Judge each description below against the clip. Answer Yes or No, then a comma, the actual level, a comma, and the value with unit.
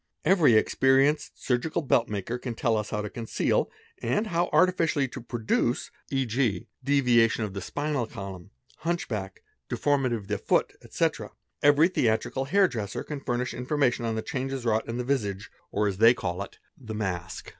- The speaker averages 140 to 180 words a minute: Yes, average, 170 wpm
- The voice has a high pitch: No, low, 120 Hz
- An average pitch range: Yes, average, 4.5 semitones